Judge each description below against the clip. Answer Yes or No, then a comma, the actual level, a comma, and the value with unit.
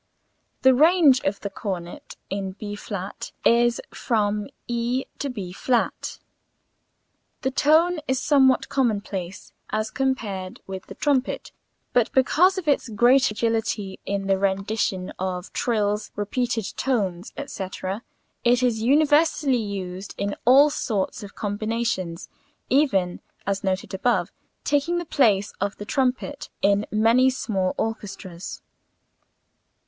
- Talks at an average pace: No, slow, 125 wpm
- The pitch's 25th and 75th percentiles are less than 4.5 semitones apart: No, average, 5.0 semitones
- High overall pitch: Yes, high, 220 Hz